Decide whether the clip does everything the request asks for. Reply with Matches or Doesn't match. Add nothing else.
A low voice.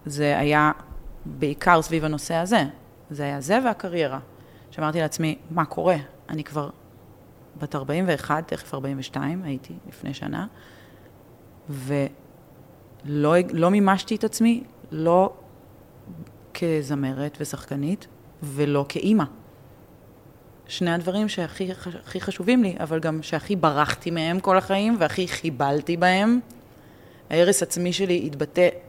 Doesn't match